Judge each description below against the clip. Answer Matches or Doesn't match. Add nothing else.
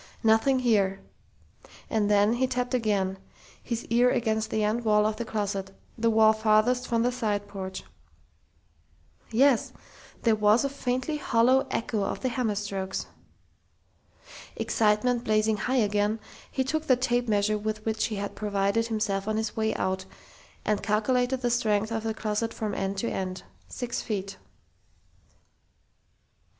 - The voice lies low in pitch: Doesn't match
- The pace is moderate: Matches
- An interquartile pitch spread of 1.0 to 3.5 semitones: Matches